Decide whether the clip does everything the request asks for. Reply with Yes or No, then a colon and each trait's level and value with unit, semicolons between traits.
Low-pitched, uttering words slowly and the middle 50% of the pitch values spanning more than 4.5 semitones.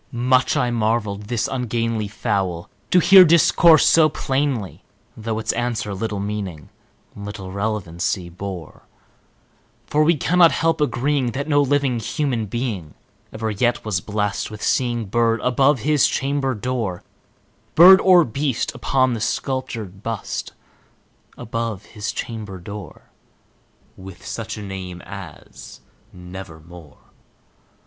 Yes: low, 115 Hz; slow, 120 wpm; average, 4.9 semitones